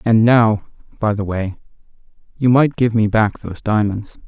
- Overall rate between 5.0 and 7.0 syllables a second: No, 4.7 syllables/s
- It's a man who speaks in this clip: Yes, male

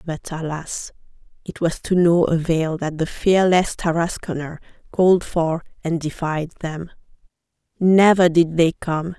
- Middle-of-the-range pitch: Yes, medium, 165 Hz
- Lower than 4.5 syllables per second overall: Yes, 4.1 syllables/s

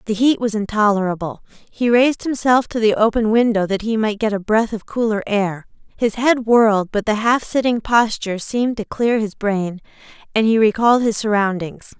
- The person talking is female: Yes, female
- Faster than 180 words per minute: Yes, average, 190 wpm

